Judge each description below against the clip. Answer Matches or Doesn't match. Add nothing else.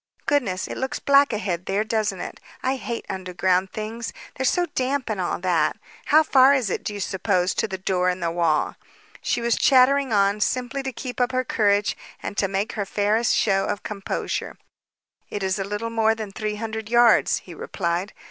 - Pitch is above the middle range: Matches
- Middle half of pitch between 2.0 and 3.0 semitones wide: Doesn't match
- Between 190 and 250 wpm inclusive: Matches